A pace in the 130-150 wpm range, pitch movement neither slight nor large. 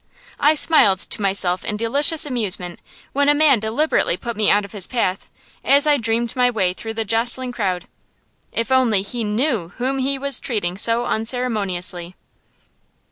No: average, 165 wpm; average, 4.7 semitones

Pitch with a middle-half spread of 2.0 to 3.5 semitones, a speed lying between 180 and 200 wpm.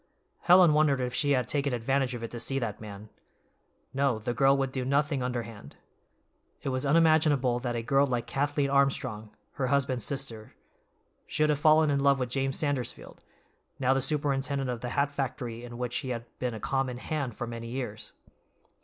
Yes: narrow, 2.5 semitones; average, 185 wpm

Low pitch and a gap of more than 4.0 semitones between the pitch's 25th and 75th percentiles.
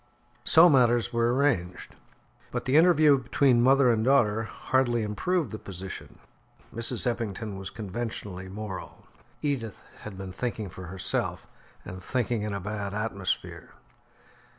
Yes: low, 115 Hz; average, 4.4 semitones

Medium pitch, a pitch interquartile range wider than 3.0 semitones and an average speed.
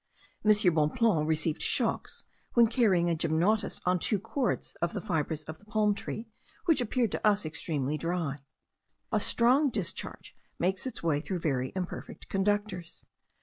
Yes: medium, 180 Hz; average, 5.2 semitones; average, 150 wpm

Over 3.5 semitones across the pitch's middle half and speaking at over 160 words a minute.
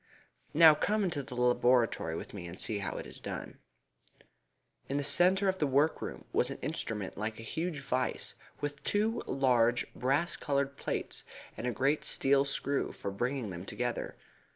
Yes: average, 3.9 semitones; average, 170 wpm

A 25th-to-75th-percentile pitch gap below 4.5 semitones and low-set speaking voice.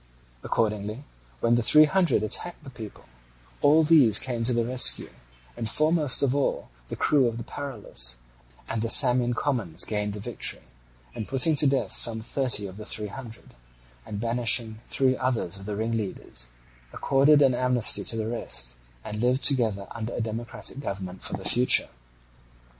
Yes: average, 3.8 semitones; low, 115 Hz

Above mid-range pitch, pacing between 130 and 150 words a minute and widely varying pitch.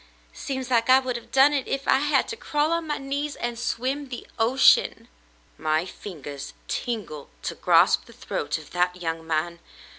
No: high, 245 Hz; average, 185 wpm; wide, 7.7 semitones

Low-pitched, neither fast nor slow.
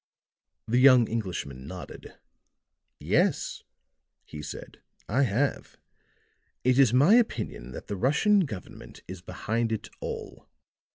No: low, 115 Hz; slow, 115 wpm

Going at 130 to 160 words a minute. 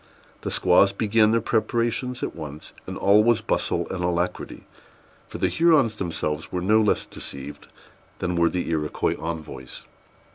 Yes: average, 150 wpm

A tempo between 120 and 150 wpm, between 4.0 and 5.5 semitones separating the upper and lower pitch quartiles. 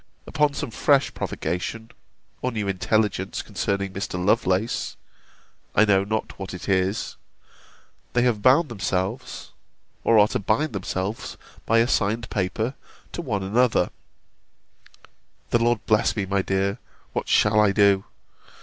No: slow, 135 wpm; average, 3.1 semitones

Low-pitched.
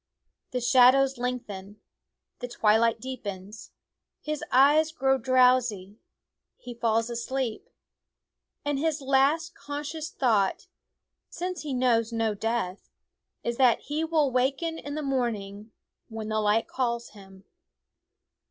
No: very high, 250 Hz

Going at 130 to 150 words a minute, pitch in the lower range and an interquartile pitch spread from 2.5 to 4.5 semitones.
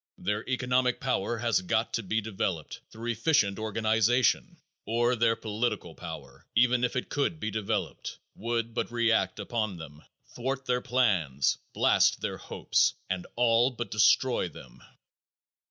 Yes: average, 140 wpm; low, 115 Hz; average, 2.9 semitones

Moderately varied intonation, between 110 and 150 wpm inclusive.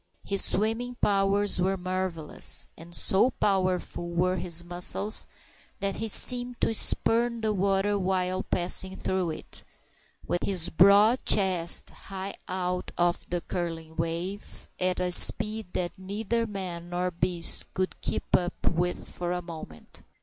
No: narrow, 2.3 semitones; average, 140 wpm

